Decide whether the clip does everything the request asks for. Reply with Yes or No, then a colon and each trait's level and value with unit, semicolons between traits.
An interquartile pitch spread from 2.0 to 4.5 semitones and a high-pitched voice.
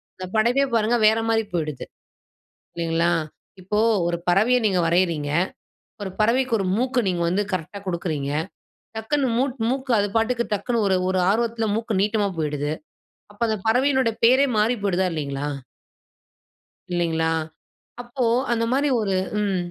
No: wide, 5.5 semitones; high, 210 Hz